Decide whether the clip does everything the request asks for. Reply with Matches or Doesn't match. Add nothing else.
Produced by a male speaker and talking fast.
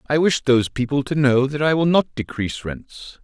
Matches